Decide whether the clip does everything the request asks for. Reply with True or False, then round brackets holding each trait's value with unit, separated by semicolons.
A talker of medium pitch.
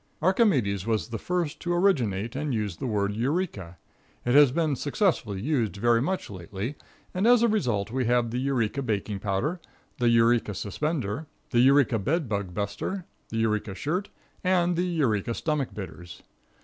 False (120 Hz)